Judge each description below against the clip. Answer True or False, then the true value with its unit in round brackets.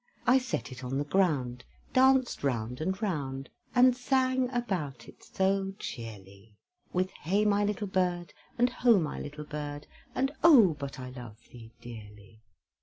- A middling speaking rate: True (155 wpm)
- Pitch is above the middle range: False (160 Hz)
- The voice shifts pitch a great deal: True (8.8 semitones)